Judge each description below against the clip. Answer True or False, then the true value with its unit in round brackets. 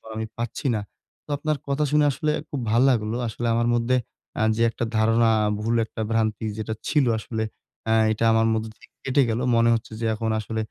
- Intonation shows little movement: True (1.9 semitones)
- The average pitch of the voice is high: False (115 Hz)